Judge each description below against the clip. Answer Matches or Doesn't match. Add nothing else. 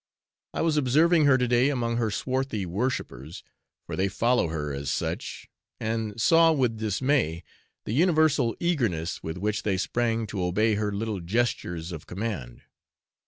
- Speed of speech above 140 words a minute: Matches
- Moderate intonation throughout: Doesn't match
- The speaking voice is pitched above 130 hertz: Doesn't match